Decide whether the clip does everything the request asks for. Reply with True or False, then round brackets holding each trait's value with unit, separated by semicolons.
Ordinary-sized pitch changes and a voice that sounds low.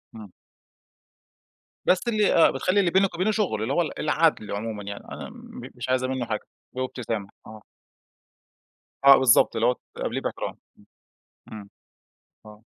False (7.8 semitones; 130 Hz)